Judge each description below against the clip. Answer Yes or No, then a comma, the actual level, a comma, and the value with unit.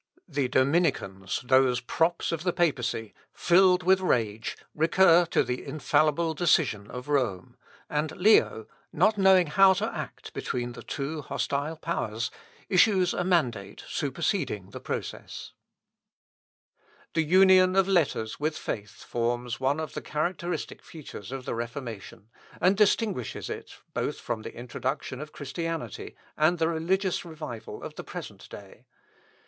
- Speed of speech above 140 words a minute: No, slow, 135 wpm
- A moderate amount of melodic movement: No, wide, 6.2 semitones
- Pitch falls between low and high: Yes, medium, 155 Hz